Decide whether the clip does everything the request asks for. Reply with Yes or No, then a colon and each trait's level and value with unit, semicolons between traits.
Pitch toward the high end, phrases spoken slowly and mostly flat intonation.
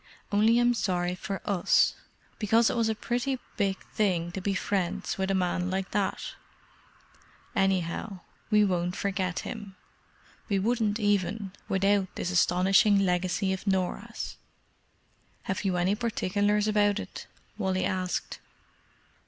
Yes: high, 195 Hz; slow, 130 wpm; narrow, 2.2 semitones